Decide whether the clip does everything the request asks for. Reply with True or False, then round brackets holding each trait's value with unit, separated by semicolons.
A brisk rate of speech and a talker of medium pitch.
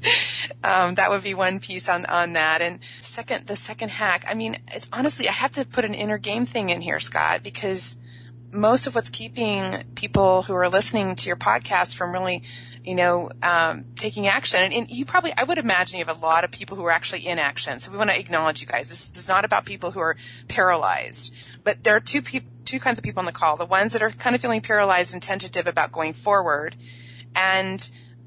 True (225 wpm; 175 Hz)